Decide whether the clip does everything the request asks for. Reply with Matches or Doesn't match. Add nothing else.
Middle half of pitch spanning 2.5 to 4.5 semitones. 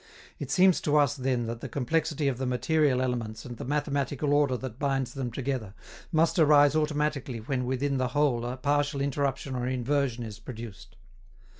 Matches